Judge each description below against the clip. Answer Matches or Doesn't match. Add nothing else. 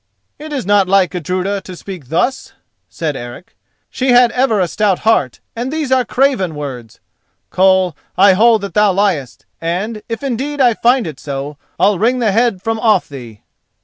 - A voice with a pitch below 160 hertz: Doesn't match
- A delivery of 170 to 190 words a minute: Matches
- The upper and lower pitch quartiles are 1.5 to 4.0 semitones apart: Doesn't match